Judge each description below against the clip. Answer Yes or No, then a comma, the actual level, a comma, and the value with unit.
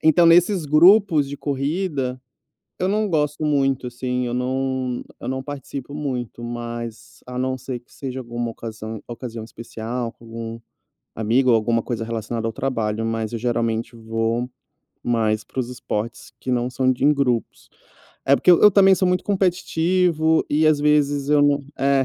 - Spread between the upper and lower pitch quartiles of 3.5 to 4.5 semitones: Yes, average, 4.2 semitones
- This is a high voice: No, low, 130 Hz